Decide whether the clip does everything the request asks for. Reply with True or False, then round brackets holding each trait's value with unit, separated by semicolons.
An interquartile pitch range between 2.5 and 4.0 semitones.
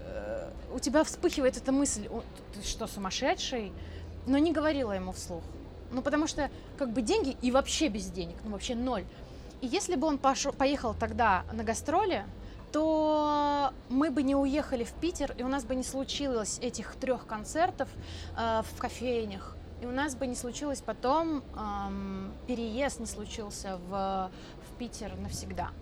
False (4.5 semitones)